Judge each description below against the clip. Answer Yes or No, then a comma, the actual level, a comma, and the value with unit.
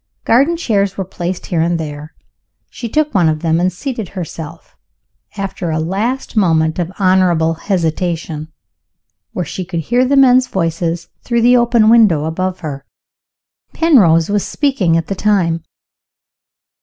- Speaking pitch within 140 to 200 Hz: Yes, medium, 185 Hz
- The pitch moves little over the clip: No, average, 5.3 semitones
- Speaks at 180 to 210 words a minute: No, average, 145 wpm